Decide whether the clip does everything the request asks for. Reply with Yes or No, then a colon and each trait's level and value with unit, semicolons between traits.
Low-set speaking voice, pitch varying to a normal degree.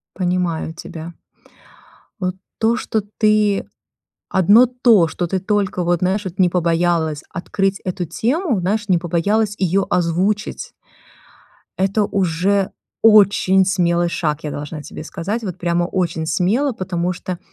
No: medium, 185 Hz; average, 3.0 semitones